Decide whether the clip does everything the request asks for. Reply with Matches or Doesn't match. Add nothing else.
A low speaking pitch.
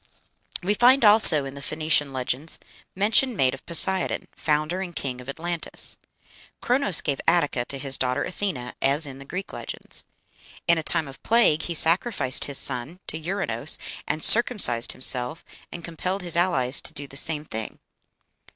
Doesn't match